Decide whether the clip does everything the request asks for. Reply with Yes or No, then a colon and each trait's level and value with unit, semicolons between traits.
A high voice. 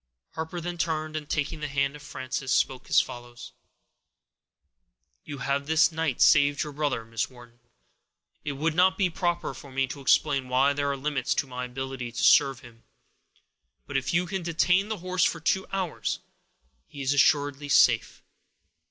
No: medium, 145 Hz